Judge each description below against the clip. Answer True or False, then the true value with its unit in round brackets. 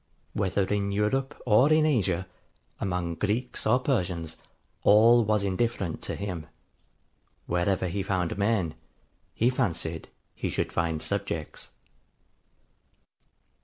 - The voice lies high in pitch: False (100 Hz)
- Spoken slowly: True (110 wpm)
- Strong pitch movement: False (4.4 semitones)